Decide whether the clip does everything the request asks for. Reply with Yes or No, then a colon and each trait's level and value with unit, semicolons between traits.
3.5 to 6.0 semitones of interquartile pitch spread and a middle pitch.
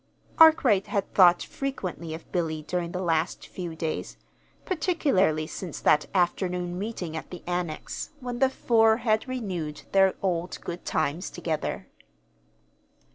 Yes: average, 4.8 semitones; medium, 180 Hz